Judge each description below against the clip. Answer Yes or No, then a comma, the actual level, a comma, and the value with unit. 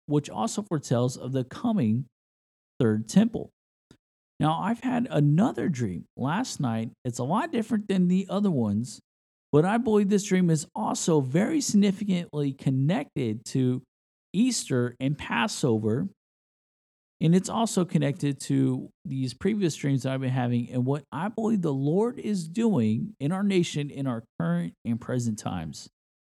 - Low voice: No, medium, 150 Hz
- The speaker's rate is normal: Yes, average, 150 wpm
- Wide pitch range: Yes, wide, 7.8 semitones